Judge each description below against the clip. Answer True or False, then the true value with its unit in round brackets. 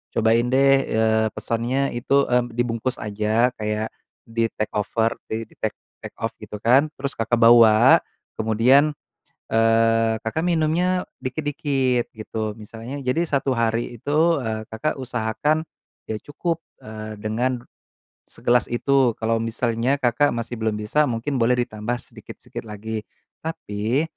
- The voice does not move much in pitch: False (3.4 semitones)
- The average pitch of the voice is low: True (115 Hz)